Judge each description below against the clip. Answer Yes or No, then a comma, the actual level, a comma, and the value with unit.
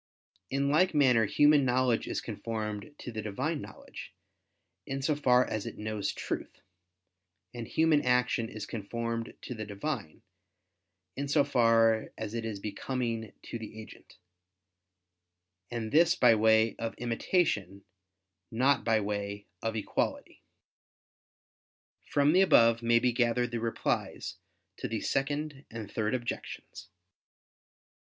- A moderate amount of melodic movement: Yes, average, 3.6 semitones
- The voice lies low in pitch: Yes, low, 115 Hz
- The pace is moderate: No, slow, 130 wpm